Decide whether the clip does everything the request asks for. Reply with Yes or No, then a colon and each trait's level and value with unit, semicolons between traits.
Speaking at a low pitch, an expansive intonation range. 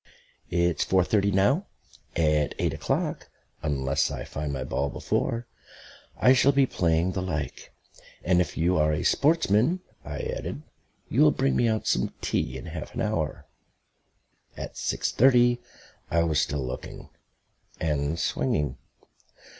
Yes: very low, 85 Hz; wide, 6.8 semitones